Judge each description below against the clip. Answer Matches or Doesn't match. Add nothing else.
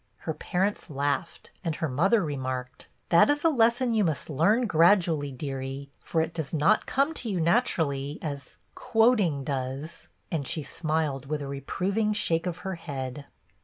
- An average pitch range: Doesn't match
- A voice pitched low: Doesn't match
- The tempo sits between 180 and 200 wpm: Matches